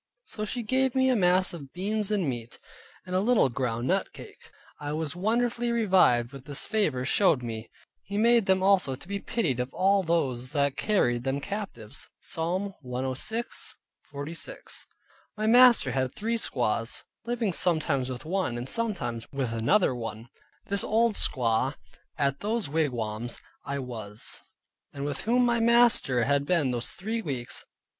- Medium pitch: Yes, medium, 160 Hz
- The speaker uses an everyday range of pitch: No, wide, 8.9 semitones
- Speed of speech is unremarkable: Yes, average, 155 wpm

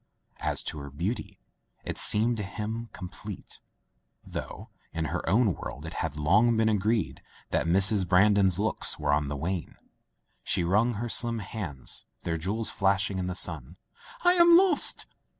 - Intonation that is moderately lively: Yes, average, 4.7 semitones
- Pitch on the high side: No, very low, 95 Hz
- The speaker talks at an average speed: Yes, average, 165 wpm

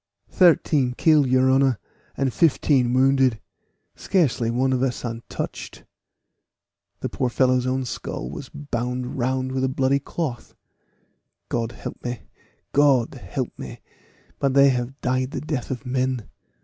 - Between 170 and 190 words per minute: No, slow, 135 wpm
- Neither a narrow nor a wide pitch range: No, narrow, 1.8 semitones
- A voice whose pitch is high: No, low, 130 Hz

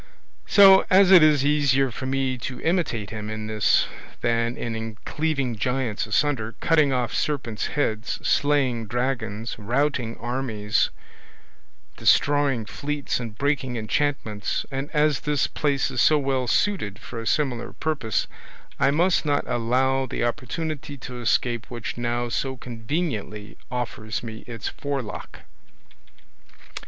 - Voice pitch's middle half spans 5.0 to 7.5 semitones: No, average, 4.1 semitones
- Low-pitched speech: Yes, low, 130 Hz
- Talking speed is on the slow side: Yes, slow, 130 wpm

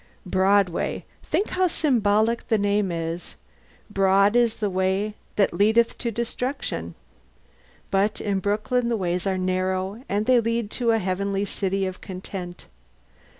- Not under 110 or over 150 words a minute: Yes, average, 140 wpm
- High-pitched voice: Yes, high, 200 Hz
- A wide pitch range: No, average, 3.2 semitones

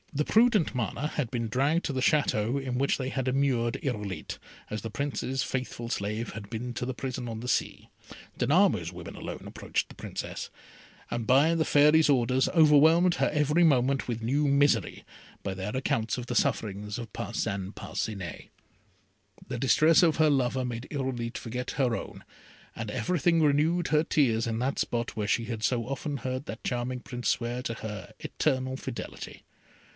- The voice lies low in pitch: Yes, low, 125 Hz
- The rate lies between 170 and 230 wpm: Yes, average, 175 wpm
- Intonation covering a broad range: No, average, 4.0 semitones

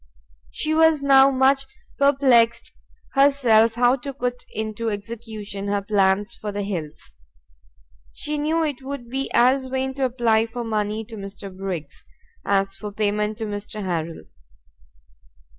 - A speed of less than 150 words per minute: Yes, average, 140 wpm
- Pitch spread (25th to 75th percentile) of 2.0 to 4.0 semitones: No, average, 4.5 semitones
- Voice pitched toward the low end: No, high, 225 Hz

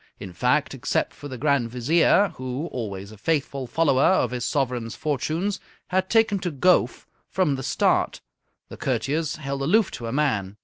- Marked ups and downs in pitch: No, average, 4.9 semitones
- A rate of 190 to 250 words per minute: No, average, 170 wpm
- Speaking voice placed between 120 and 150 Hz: Yes, medium, 140 Hz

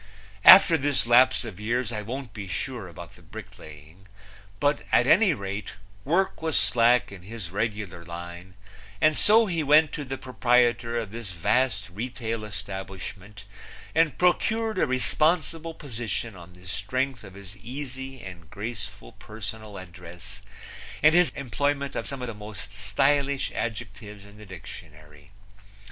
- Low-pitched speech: Yes, low, 110 Hz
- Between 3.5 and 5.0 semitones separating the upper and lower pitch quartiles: No, wide, 5.5 semitones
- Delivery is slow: No, average, 145 wpm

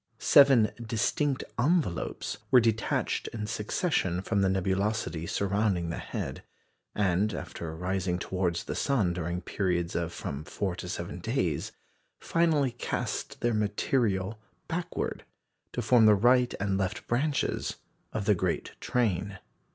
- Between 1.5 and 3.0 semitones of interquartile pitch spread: No, average, 4.9 semitones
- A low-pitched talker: Yes, low, 105 Hz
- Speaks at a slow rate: Yes, slow, 130 wpm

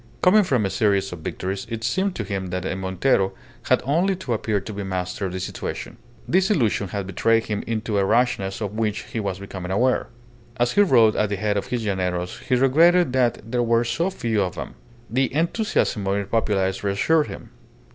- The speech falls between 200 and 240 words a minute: Yes, fast, 205 wpm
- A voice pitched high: No, low, 110 Hz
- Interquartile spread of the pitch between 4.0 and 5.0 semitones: Yes, average, 4.6 semitones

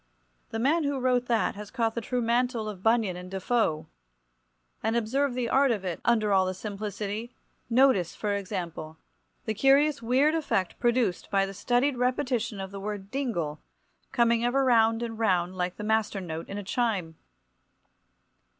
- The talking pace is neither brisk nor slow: Yes, average, 165 wpm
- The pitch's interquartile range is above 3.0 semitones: Yes, average, 4.1 semitones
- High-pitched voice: Yes, high, 225 Hz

